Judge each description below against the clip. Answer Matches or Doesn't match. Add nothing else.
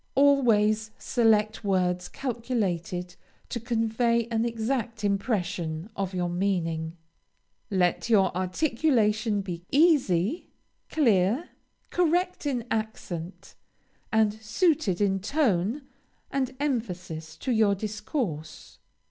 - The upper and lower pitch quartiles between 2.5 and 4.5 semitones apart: Doesn't match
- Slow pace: Matches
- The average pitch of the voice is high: Matches